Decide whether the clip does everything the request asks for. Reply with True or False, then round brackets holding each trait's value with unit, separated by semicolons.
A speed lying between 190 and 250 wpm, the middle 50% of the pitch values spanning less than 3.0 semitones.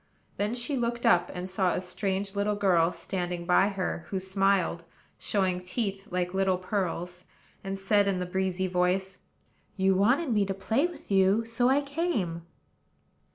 False (160 wpm; 2.4 semitones)